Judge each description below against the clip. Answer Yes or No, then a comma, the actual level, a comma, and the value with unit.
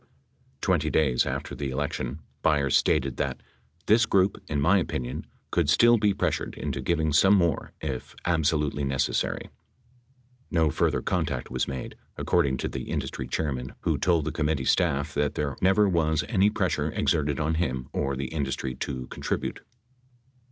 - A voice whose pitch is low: Yes, very low, 75 Hz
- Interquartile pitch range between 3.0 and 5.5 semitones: Yes, average, 4.0 semitones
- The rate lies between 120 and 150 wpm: No, average, 160 wpm